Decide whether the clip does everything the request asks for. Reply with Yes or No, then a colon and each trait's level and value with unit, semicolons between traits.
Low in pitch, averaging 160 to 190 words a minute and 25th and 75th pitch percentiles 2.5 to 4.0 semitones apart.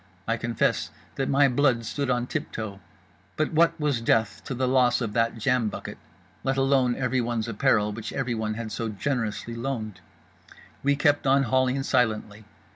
Yes: low, 120 Hz; average, 165 wpm; average, 3.1 semitones